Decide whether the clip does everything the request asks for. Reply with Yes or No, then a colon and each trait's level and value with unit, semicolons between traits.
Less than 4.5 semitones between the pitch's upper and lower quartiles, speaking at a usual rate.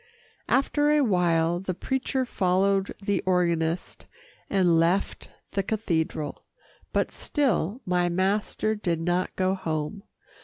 No: average, 3.2 semitones; slow, 115 wpm